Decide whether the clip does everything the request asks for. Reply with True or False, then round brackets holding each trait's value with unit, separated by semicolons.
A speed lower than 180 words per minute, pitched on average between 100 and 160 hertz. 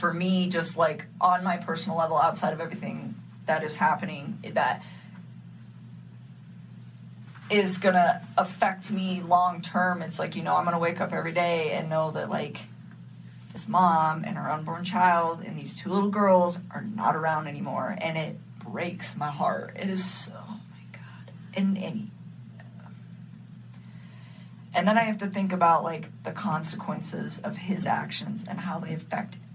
False (160 wpm; 170 Hz)